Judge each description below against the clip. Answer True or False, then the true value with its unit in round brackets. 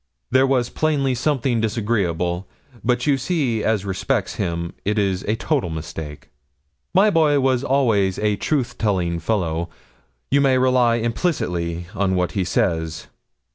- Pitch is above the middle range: False (110 Hz)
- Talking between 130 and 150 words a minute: True (140 wpm)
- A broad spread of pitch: True (6.6 semitones)